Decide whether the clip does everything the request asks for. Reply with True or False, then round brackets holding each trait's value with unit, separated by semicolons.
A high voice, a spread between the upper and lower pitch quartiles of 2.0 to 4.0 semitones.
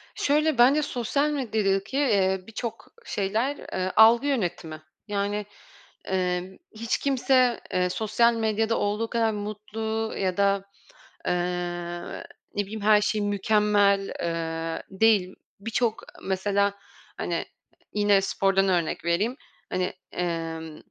True (205 Hz; 3.0 semitones)